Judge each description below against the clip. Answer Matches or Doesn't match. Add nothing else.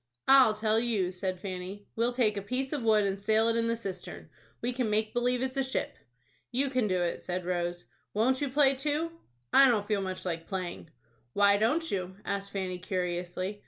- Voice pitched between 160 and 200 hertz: Doesn't match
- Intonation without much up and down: Doesn't match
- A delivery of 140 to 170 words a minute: Doesn't match